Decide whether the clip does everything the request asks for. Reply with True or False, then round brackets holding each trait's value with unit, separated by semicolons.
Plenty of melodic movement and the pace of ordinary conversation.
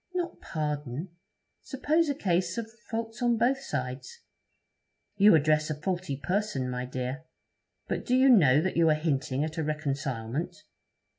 True (8.2 semitones; 150 wpm)